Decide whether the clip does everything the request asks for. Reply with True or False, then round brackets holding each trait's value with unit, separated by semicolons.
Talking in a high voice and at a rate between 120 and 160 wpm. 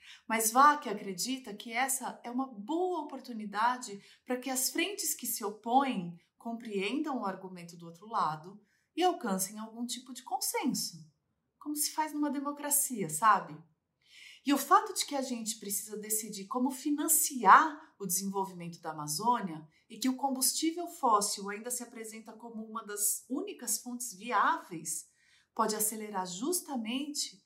True (235 Hz; 150 wpm)